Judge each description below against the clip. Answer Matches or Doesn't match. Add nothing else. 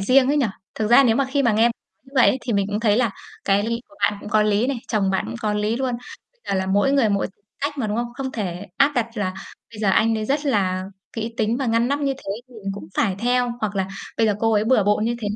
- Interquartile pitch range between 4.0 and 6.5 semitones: Doesn't match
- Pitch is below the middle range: Doesn't match